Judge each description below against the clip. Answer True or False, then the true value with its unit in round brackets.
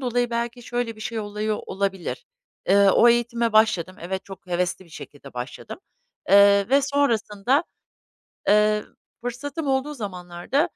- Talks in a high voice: True (215 Hz)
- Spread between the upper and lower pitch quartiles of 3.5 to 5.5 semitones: True (4.1 semitones)